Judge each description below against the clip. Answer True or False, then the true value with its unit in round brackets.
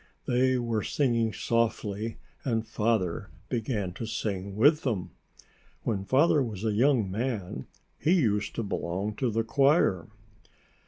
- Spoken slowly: True (130 wpm)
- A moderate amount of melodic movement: True (3.7 semitones)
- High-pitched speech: False (115 Hz)